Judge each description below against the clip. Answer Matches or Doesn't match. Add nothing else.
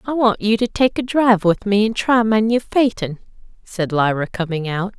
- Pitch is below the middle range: Doesn't match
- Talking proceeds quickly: Matches